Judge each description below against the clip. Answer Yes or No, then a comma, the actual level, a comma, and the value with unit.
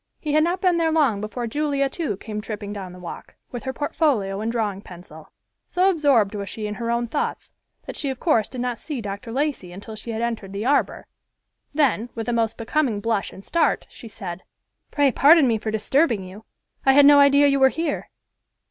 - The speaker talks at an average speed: No, fast, 210 wpm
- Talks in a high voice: Yes, high, 235 Hz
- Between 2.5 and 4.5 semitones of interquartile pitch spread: No, wide, 5.4 semitones